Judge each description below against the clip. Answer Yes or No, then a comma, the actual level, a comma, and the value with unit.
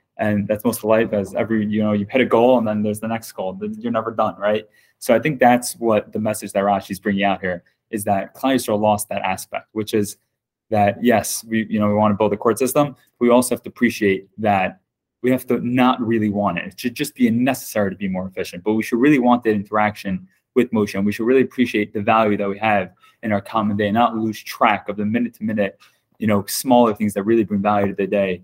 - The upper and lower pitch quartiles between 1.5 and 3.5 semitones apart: Yes, narrow, 2.6 semitones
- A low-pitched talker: Yes, low, 110 Hz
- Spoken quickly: Yes, fast, 250 wpm